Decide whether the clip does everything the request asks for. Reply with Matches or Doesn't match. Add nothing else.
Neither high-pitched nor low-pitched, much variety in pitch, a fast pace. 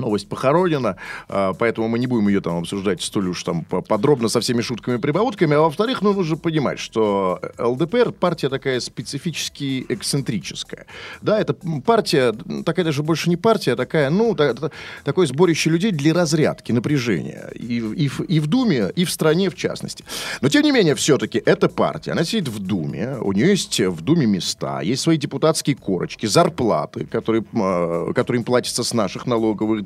Matches